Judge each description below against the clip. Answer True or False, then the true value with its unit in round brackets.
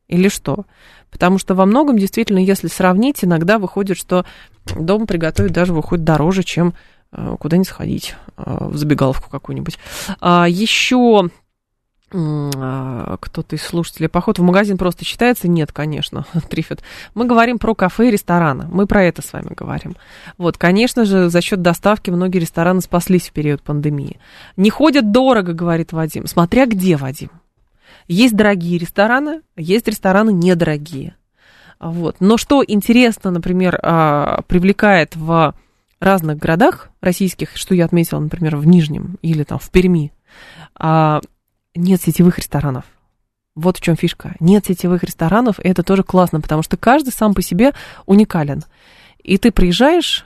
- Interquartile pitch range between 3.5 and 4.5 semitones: True (3.8 semitones)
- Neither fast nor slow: True (140 wpm)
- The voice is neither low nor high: True (180 Hz)